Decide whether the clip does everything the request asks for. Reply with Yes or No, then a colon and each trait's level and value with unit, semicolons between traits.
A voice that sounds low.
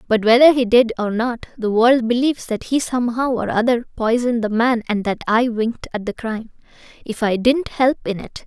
No: high, 235 Hz